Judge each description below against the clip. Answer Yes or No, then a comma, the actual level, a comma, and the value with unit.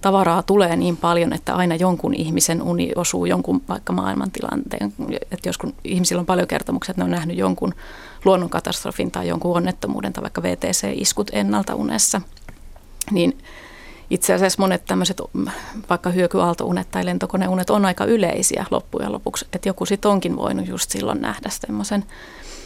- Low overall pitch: No, medium, 175 Hz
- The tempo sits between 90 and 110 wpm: No, average, 150 wpm